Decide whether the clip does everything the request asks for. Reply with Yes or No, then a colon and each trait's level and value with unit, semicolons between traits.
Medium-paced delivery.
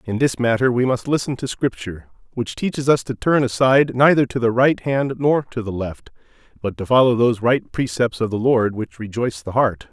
No: fast, 220 wpm